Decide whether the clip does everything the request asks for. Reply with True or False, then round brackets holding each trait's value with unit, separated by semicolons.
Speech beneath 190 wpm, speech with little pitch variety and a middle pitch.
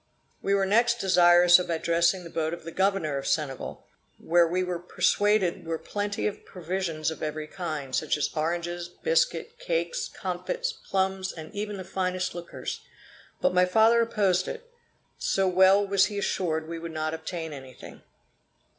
False (165 wpm; 3.4 semitones; 180 Hz)